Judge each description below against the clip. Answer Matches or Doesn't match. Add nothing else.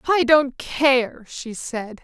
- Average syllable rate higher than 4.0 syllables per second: Doesn't match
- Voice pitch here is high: Matches